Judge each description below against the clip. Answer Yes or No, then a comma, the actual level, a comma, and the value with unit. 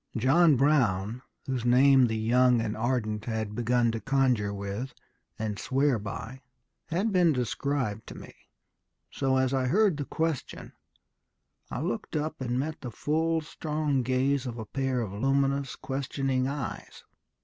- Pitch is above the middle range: No, low, 130 Hz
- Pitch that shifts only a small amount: No, average, 3.5 semitones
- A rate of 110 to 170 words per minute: Yes, average, 150 wpm